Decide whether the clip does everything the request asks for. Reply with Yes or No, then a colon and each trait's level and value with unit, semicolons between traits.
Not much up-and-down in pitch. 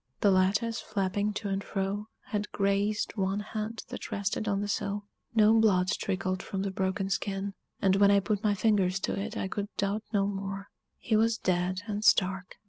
Yes: narrow, 1.4 semitones